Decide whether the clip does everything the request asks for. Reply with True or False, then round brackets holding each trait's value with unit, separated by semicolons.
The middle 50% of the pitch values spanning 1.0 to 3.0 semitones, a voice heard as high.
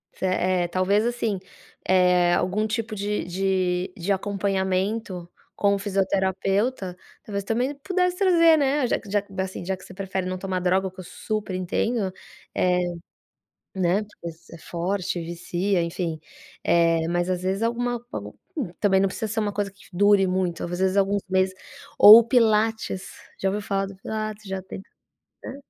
True (2.5 semitones; 195 Hz)